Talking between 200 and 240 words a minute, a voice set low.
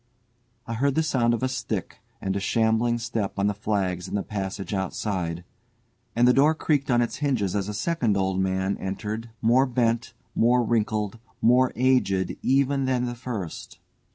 No: average, 175 wpm; low, 115 Hz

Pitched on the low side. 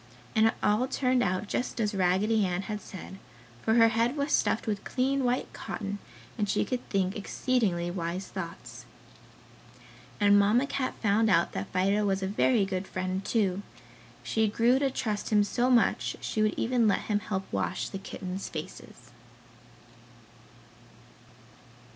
No: high, 205 Hz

